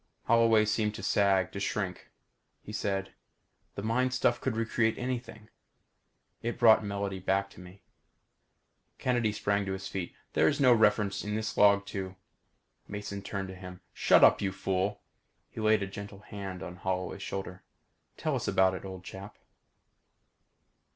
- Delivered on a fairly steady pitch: Yes, narrow, 2.3 semitones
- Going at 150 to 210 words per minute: Yes, average, 160 wpm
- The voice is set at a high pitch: No, low, 100 Hz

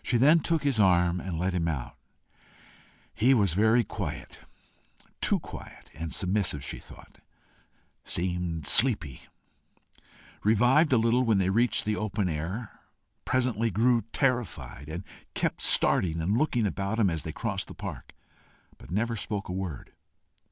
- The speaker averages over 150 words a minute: No, average, 145 wpm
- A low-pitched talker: Yes, low, 105 Hz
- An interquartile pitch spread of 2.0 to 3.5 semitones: No, average, 5.1 semitones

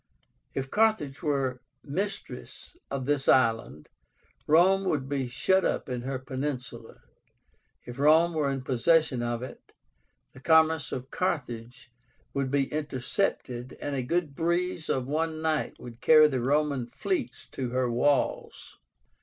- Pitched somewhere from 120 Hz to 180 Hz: Yes, medium, 140 Hz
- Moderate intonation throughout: Yes, average, 3.8 semitones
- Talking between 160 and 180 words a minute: No, slow, 135 wpm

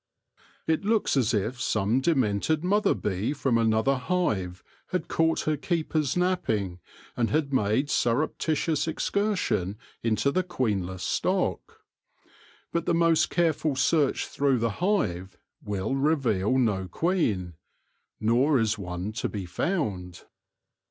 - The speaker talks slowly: Yes, slow, 130 wpm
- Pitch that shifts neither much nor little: No, wide, 7.7 semitones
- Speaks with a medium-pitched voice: No, low, 130 Hz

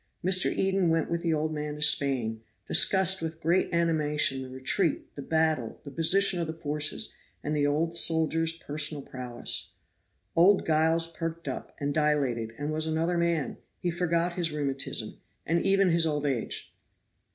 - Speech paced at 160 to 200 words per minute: Yes, average, 165 wpm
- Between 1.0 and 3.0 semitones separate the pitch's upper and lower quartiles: Yes, narrow, 2.5 semitones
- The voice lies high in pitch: No, medium, 160 Hz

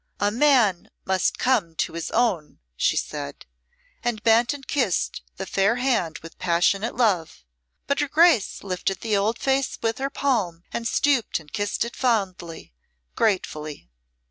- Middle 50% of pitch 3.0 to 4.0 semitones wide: No, wide, 5.6 semitones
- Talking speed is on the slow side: No, average, 150 wpm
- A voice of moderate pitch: No, high, 215 Hz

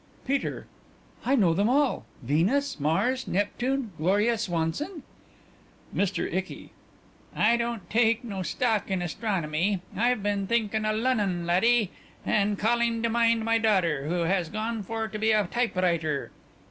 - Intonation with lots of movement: No, average, 4.3 semitones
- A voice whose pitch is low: No, high, 215 Hz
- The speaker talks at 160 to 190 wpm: No, average, 140 wpm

